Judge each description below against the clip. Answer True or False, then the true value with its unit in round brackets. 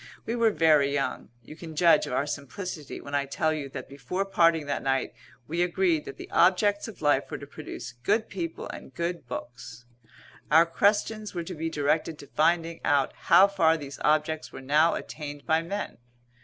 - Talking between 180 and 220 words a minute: True (190 wpm)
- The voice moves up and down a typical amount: True (3.5 semitones)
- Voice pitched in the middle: True (160 Hz)